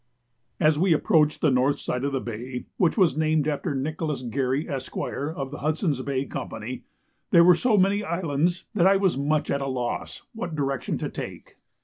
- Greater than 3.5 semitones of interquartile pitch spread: Yes, average, 4.0 semitones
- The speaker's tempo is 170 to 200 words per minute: Yes, average, 190 wpm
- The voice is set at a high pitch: No, medium, 150 Hz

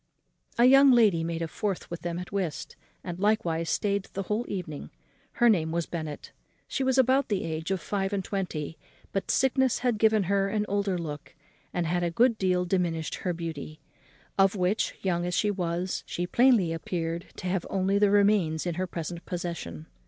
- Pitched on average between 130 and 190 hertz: Yes, medium, 185 Hz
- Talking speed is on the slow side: No, average, 190 wpm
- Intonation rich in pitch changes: No, average, 3.5 semitones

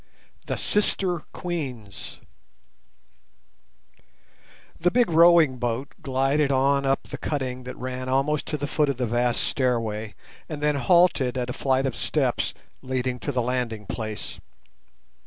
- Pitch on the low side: Yes, low, 130 Hz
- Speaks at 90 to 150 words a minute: Yes, average, 140 wpm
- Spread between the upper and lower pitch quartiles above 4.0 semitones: No, average, 3.2 semitones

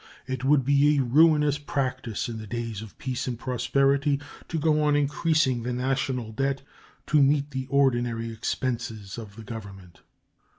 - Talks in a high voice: No, low, 130 Hz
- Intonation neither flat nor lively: Yes, average, 3.5 semitones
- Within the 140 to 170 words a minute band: Yes, average, 160 wpm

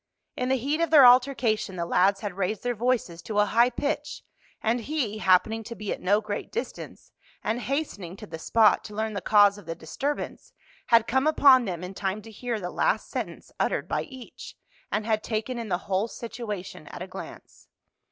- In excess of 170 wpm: Yes, average, 200 wpm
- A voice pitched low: No, high, 220 Hz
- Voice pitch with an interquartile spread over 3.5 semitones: Yes, average, 4.1 semitones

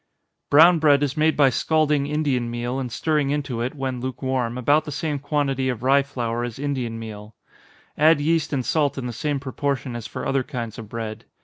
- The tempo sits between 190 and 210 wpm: Yes, fast, 205 wpm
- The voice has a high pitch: No, low, 135 Hz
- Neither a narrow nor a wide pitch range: Yes, average, 3.4 semitones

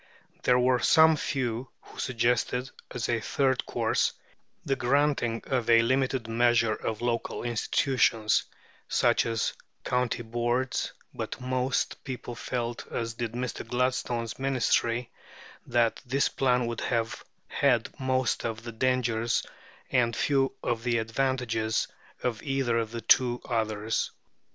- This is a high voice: No, low, 120 Hz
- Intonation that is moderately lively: No, narrow, 2.0 semitones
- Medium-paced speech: No, slow, 130 wpm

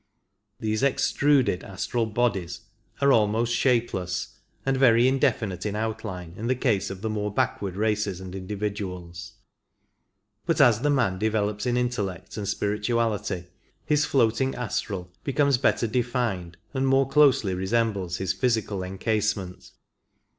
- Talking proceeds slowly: Yes, slow, 130 wpm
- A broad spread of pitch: No, average, 4.4 semitones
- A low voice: Yes, low, 110 Hz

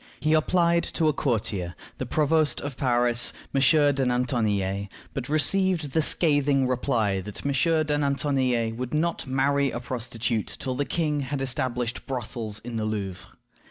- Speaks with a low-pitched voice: Yes, low, 130 Hz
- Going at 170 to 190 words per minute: No, average, 155 wpm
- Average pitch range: Yes, average, 3.9 semitones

